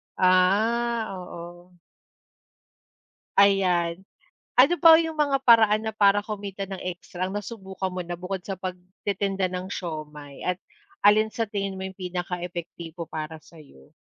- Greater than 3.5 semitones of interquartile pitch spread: No, average, 2.7 semitones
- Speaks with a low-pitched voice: No, high, 190 Hz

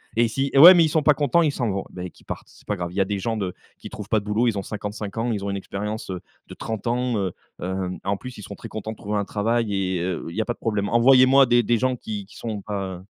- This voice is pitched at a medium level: No, low, 105 Hz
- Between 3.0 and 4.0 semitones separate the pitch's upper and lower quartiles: Yes, average, 3.5 semitones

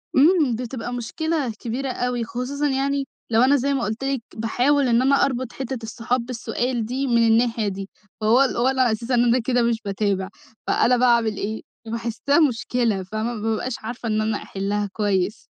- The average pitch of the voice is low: No, high, 240 Hz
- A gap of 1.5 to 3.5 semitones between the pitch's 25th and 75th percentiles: Yes, average, 2.7 semitones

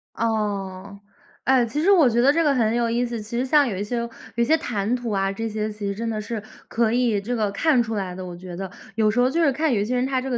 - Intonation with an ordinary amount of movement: Yes, average, 3.4 semitones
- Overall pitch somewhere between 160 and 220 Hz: No, high, 230 Hz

